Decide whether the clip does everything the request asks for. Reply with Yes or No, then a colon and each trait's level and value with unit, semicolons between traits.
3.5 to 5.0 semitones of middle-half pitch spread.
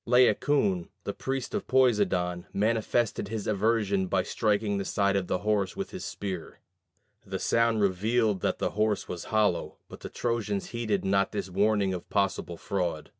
No: average, 2.8 semitones